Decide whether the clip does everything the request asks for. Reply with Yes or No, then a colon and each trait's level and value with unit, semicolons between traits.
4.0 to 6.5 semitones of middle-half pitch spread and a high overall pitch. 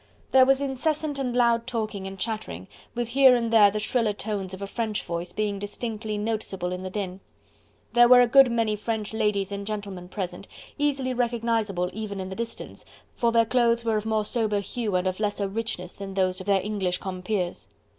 No: average, 3.3 semitones; high, 215 Hz